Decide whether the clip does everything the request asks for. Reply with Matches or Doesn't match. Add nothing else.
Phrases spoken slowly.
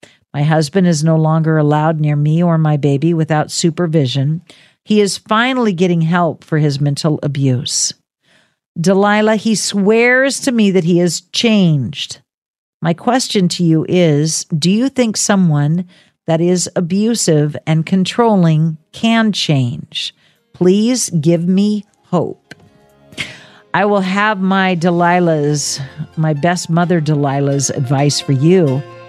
Matches